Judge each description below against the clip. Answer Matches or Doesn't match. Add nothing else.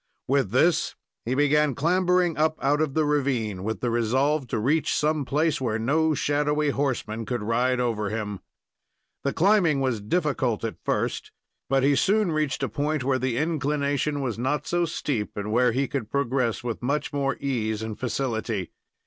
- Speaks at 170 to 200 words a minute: Matches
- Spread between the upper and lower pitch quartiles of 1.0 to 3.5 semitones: Doesn't match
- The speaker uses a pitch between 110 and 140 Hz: Matches